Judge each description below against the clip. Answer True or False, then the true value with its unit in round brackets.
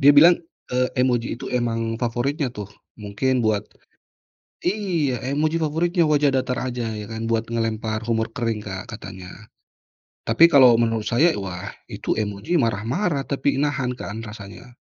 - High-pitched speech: False (120 Hz)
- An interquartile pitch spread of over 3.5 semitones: True (4.3 semitones)